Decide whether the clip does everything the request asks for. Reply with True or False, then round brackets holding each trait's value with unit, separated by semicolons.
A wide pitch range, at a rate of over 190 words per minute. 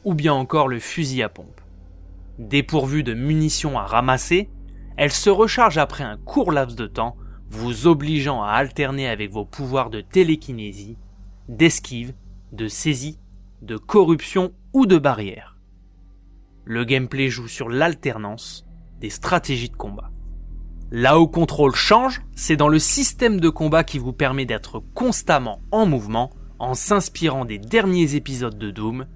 False (6.8 semitones; 145 wpm)